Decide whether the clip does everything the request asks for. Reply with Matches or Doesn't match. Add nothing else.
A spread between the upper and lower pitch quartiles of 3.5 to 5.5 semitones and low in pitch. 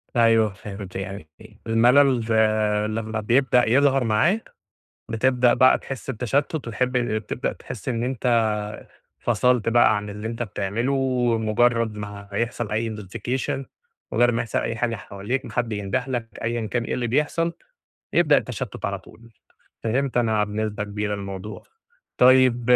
Doesn't match